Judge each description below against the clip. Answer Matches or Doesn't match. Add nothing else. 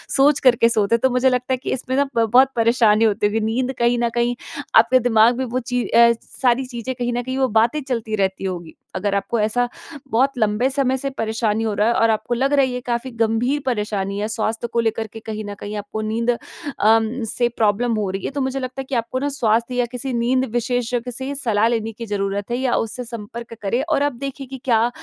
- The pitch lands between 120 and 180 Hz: Doesn't match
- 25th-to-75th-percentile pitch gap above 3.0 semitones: Doesn't match